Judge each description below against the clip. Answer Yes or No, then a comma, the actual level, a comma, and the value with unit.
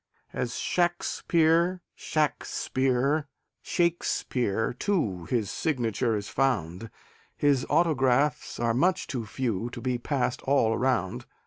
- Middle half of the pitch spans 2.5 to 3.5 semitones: No, average, 5.2 semitones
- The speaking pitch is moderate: No, low, 130 Hz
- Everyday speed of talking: No, slow, 105 wpm